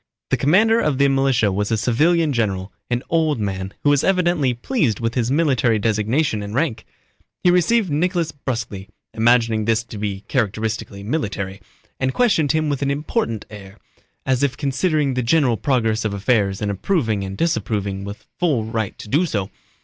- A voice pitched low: Yes, low, 120 Hz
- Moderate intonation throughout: No, wide, 5.9 semitones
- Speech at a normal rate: Yes, average, 170 wpm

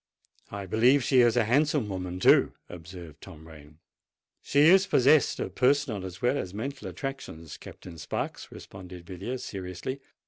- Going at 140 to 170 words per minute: Yes, average, 150 wpm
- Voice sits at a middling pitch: No, low, 105 Hz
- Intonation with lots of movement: Yes, wide, 7.0 semitones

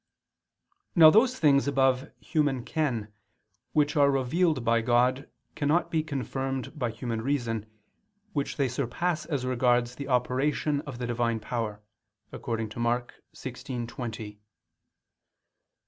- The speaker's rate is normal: No, slow, 125 wpm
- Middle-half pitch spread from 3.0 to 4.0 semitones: Yes, average, 3.5 semitones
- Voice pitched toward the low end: Yes, low, 130 Hz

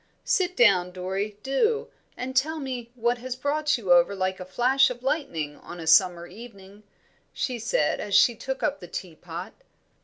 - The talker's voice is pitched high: Yes, high, 230 Hz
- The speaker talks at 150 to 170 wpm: No, average, 180 wpm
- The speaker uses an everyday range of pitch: No, wide, 6.3 semitones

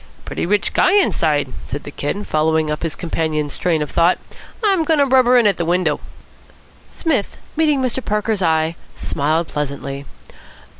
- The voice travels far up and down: Yes, wide, 8.1 semitones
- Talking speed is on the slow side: No, average, 160 wpm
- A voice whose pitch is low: No, medium, 170 Hz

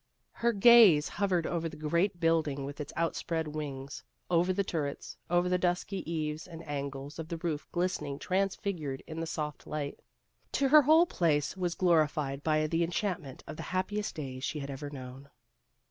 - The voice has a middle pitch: Yes, medium, 160 Hz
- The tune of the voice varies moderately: Yes, average, 3.6 semitones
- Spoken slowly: No, average, 175 wpm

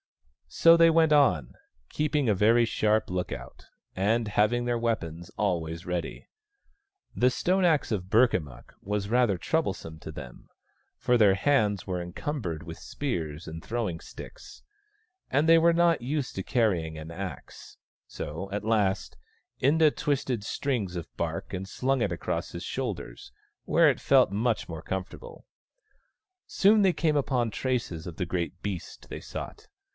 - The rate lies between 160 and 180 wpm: No, average, 150 wpm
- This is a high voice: No, low, 105 Hz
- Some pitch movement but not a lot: No, wide, 7.6 semitones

